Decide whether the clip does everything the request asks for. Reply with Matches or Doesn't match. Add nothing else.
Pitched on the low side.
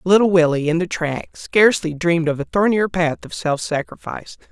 Doesn't match